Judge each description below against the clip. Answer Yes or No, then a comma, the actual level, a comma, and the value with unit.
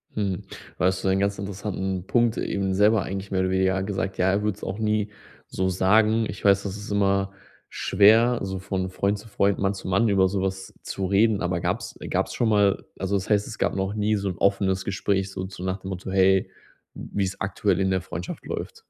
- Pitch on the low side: Yes, very low, 95 Hz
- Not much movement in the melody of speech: Yes, narrow, 1.3 semitones